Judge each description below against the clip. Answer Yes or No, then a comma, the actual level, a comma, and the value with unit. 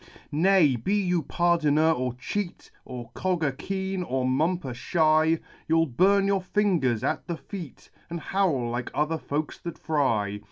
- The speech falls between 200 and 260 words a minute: No, average, 150 wpm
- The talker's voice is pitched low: No, medium, 160 Hz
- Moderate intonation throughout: No, wide, 5.7 semitones